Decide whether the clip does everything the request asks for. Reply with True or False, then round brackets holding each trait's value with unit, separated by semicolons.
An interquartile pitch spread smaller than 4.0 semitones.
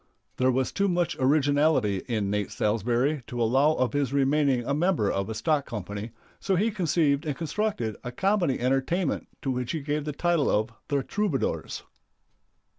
False (4.5 semitones)